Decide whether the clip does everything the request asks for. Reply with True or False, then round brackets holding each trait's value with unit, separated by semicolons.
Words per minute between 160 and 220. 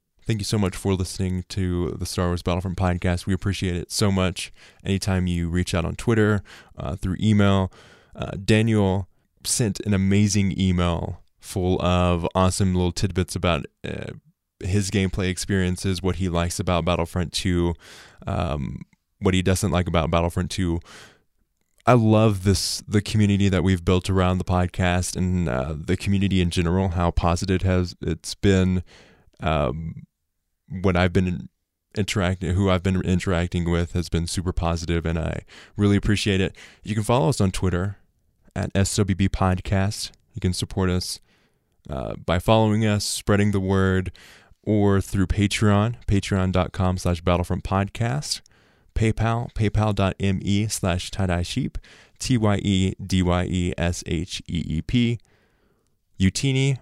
False (150 wpm)